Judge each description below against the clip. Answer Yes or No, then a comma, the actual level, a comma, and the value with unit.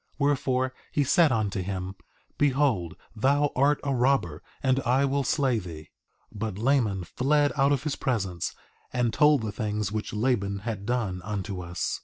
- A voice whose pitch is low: Yes, low, 120 Hz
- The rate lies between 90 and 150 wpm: No, average, 165 wpm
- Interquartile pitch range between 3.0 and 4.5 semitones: No, wide, 5.6 semitones